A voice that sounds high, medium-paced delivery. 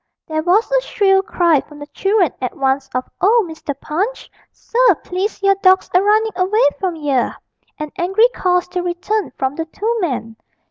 Yes: very high, 360 Hz; average, 180 wpm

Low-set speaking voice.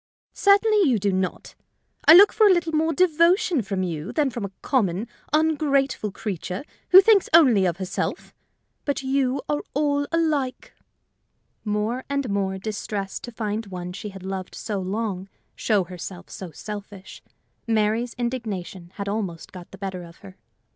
No: high, 215 Hz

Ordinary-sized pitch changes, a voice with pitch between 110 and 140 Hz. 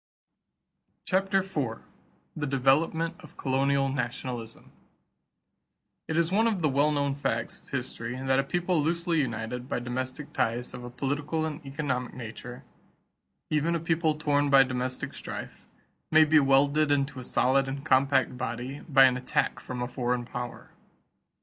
Yes: average, 3.4 semitones; low, 135 Hz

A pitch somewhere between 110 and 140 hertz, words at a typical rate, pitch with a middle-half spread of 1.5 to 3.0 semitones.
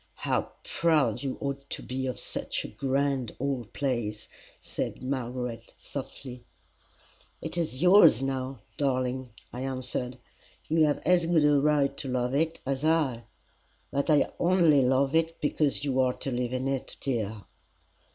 Yes: low, 135 Hz; average, 150 wpm; average, 2.7 semitones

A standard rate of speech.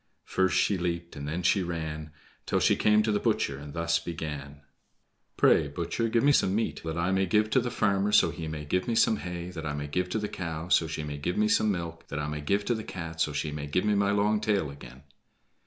No: fast, 255 wpm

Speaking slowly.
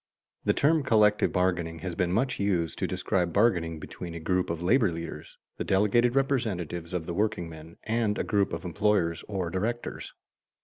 No: average, 175 wpm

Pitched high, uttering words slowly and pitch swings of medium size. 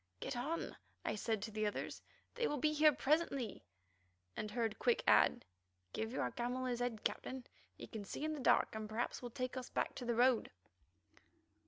No: high, 245 Hz; average, 190 wpm; average, 3.9 semitones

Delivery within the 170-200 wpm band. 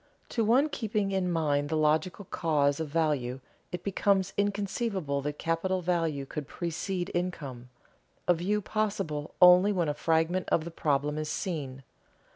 No: average, 150 wpm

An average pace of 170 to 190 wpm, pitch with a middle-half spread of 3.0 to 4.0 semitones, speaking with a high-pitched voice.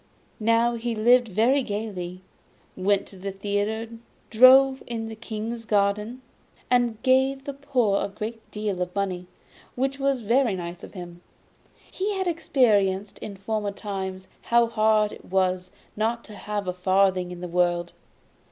No: average, 150 wpm; average, 3.7 semitones; high, 215 Hz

